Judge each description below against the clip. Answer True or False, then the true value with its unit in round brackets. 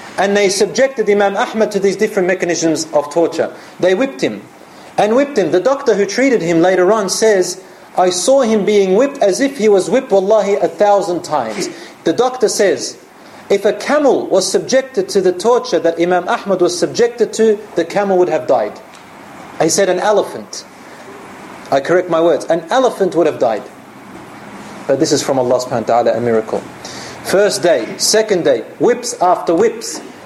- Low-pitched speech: False (195 Hz)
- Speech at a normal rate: True (180 wpm)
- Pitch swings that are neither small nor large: True (4.0 semitones)